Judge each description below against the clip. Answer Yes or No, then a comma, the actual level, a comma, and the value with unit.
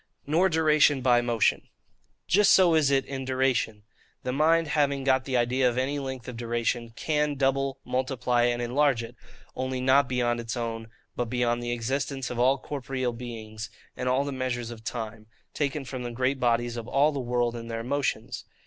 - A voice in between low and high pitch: No, low, 130 Hz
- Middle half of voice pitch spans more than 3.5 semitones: No, narrow, 2.5 semitones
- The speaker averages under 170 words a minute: No, average, 185 wpm